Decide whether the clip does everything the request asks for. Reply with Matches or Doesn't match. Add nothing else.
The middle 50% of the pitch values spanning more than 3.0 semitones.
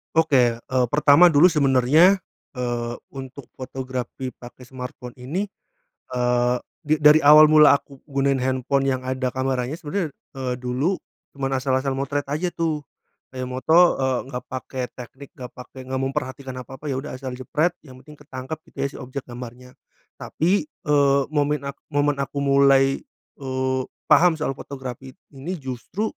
Doesn't match